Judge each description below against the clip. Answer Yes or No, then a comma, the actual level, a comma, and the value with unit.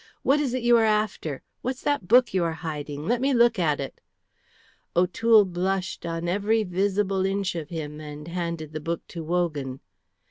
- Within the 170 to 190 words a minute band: Yes, average, 180 wpm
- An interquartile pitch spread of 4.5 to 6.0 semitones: Yes, average, 5.2 semitones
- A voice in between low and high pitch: Yes, medium, 180 Hz